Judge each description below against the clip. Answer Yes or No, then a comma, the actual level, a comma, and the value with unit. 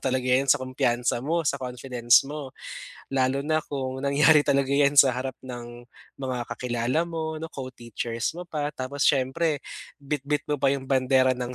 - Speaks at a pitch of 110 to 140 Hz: Yes, low, 135 Hz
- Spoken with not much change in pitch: Yes, narrow, 2.3 semitones